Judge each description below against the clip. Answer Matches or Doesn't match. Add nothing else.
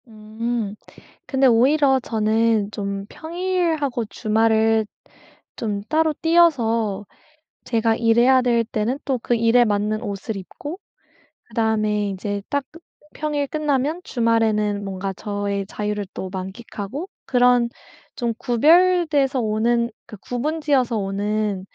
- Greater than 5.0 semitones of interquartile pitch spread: Doesn't match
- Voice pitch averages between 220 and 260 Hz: Matches